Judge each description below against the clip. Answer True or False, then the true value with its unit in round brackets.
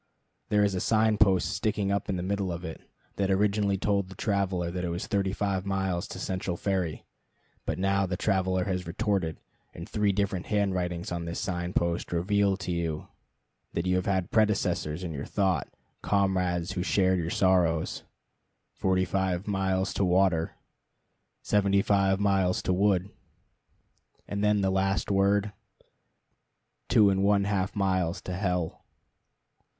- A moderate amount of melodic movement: False (1.8 semitones)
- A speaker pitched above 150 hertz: False (95 Hz)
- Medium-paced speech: True (155 wpm)